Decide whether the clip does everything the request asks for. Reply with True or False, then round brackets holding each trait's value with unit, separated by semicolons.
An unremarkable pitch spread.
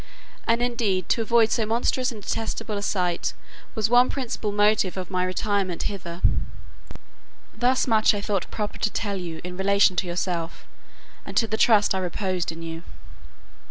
True (3.4 semitones)